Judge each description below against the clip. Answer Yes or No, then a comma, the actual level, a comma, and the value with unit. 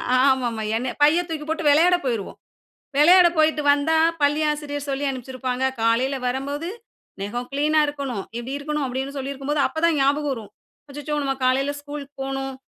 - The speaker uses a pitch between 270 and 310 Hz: Yes, very high, 280 Hz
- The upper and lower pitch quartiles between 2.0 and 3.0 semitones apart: Yes, narrow, 2.4 semitones